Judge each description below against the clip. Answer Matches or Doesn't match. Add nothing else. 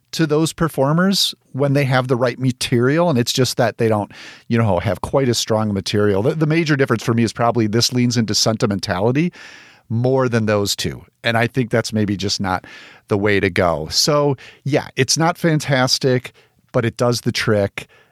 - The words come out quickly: Doesn't match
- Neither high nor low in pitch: Doesn't match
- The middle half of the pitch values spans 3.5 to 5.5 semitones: Matches